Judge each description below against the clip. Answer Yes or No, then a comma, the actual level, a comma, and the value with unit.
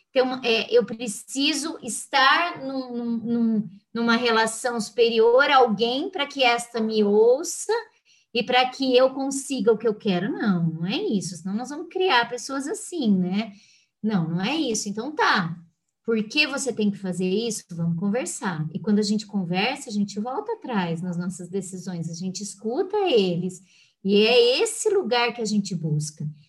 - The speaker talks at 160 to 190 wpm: Yes, average, 170 wpm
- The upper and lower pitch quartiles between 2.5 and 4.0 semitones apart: No, wide, 5.6 semitones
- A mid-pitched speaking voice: No, high, 225 Hz